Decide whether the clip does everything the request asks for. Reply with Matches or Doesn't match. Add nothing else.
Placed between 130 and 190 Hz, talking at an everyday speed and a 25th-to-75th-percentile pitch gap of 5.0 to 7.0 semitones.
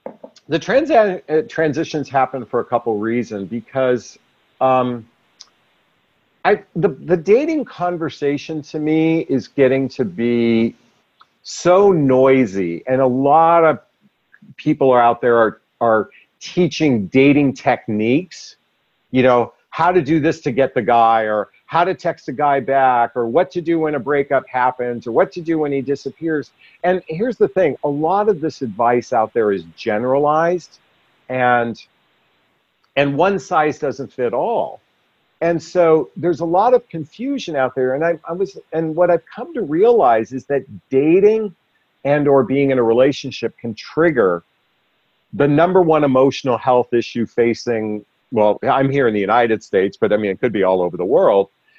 Matches